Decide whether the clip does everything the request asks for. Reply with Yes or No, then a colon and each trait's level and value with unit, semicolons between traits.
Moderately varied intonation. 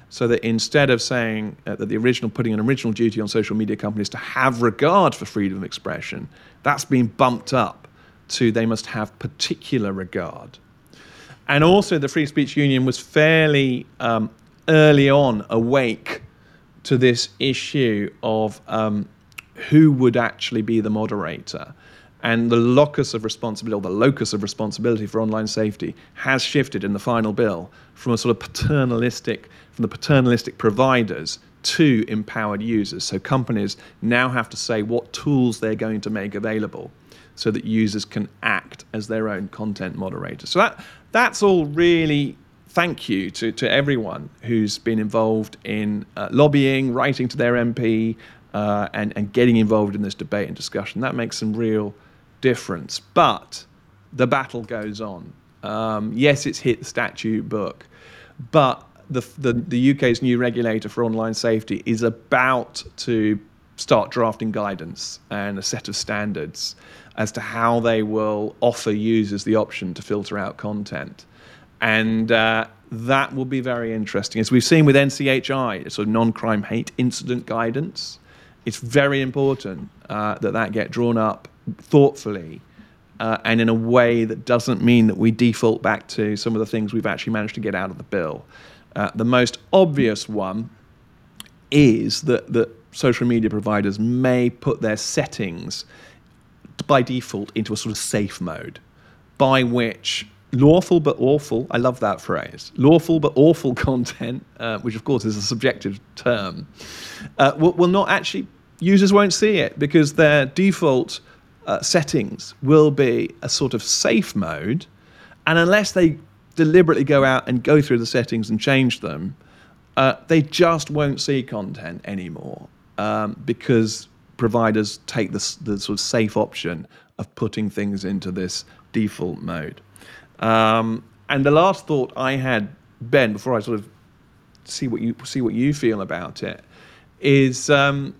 Yes: average, 3.6 semitones